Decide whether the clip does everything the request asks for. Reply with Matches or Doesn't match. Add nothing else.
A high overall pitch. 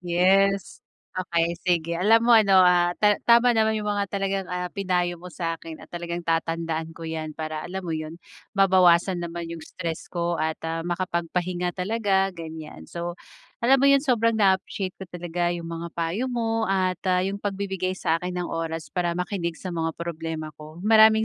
Doesn't match